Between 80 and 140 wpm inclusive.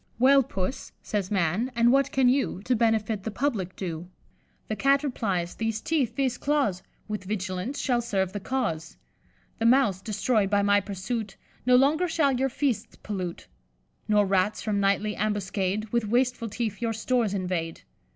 No: average, 160 wpm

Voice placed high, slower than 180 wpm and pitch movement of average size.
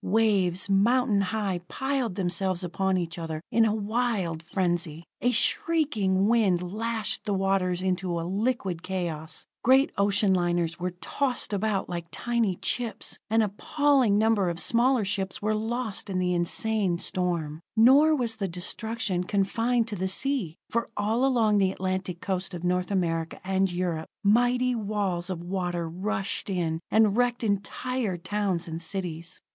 Yes: high, 195 Hz; average, 150 wpm; average, 4.0 semitones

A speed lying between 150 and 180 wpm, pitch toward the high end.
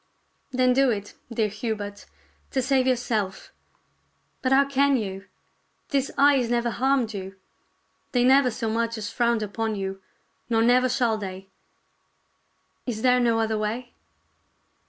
No: slow, 135 wpm; high, 235 Hz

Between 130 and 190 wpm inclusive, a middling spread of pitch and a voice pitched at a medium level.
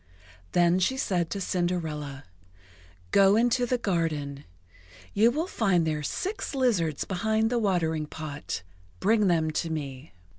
No: slow, 135 wpm; wide, 5.9 semitones; medium, 175 Hz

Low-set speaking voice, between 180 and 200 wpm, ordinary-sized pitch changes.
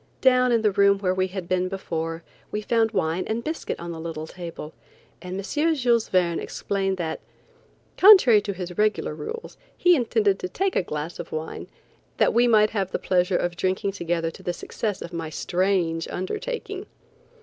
No: high, 190 Hz; average, 185 wpm; average, 4.4 semitones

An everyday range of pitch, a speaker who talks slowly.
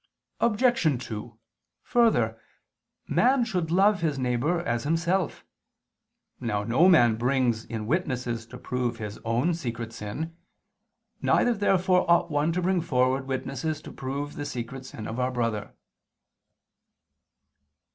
No: wide, 6.4 semitones; slow, 125 wpm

